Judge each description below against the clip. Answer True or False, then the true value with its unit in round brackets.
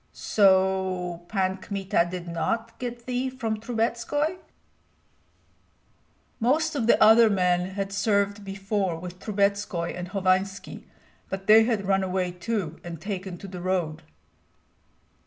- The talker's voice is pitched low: False (195 Hz)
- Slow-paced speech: True (125 wpm)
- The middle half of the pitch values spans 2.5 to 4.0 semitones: True (3.3 semitones)